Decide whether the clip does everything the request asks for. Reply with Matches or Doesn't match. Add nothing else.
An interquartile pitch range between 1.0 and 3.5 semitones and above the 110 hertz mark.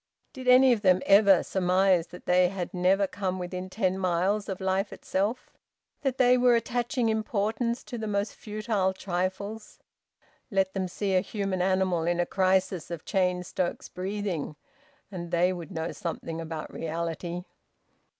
Matches